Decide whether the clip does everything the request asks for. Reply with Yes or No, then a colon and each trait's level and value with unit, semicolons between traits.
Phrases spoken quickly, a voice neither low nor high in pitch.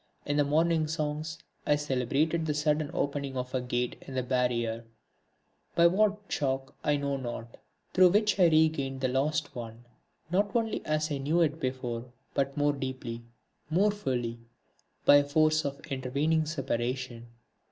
No: average, 155 wpm; medium, 145 Hz